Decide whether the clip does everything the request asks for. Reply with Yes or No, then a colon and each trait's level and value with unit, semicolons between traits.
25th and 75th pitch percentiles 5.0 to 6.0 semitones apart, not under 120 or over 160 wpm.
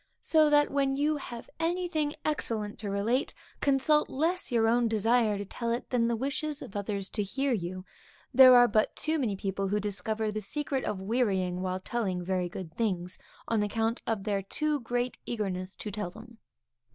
No: average, 5.3 semitones; average, 185 wpm